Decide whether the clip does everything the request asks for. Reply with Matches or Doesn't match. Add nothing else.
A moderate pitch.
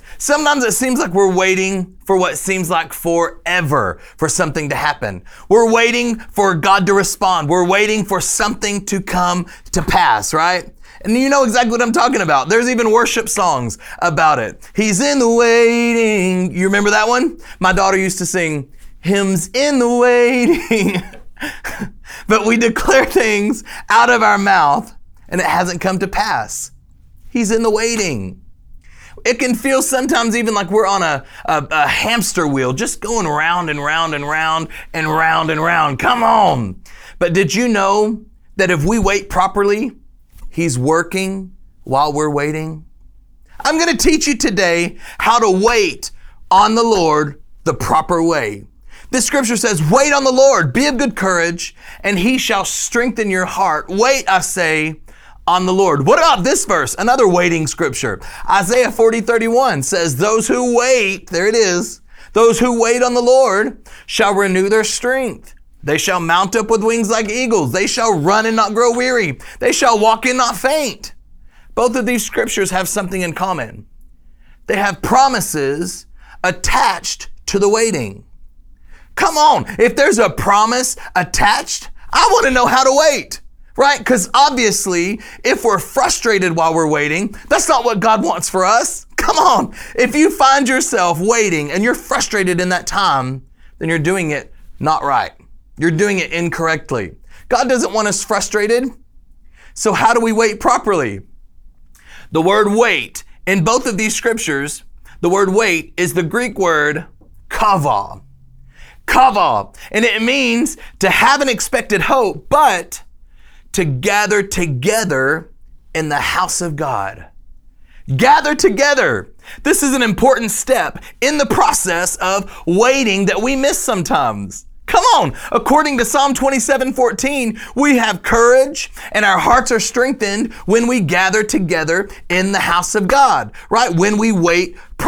Doesn't match